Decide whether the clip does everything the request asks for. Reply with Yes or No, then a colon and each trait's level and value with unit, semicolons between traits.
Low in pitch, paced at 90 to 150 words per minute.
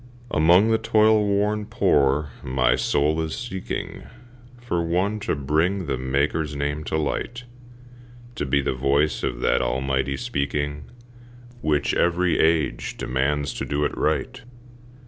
Yes: very low, 75 Hz; slow, 135 wpm